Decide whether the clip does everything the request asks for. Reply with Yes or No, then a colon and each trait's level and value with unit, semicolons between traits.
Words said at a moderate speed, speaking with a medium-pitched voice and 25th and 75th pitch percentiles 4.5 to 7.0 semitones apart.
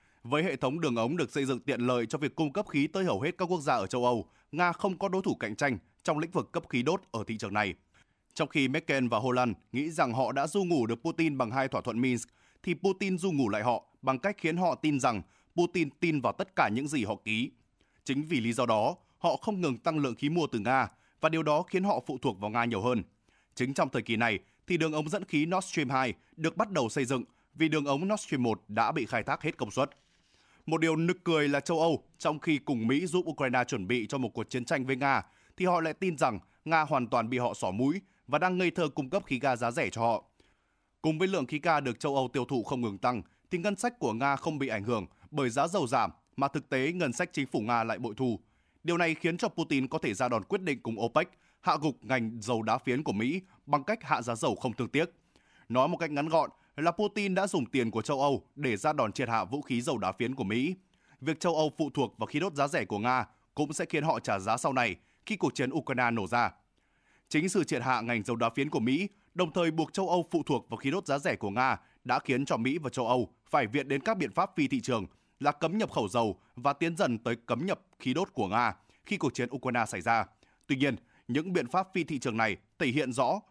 No: fast, 265 wpm; medium, 145 Hz; wide, 5.4 semitones